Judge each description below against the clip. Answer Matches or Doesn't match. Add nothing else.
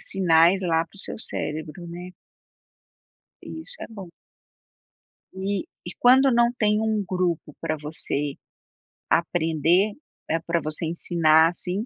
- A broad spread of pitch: Doesn't match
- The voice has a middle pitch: Matches